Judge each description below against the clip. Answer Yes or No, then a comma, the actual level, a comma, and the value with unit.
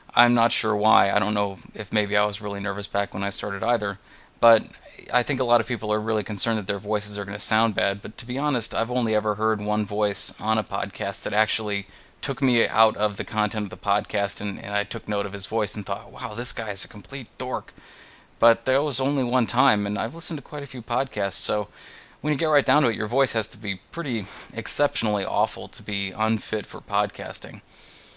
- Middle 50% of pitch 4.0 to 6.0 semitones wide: No, narrow, 2.4 semitones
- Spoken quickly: Yes, fast, 240 wpm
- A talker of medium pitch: No, low, 105 Hz